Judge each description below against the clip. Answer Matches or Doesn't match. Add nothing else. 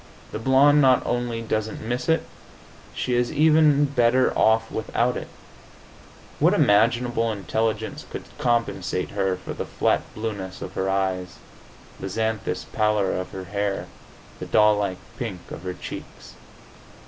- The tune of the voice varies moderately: Matches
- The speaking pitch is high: Doesn't match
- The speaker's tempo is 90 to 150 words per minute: Matches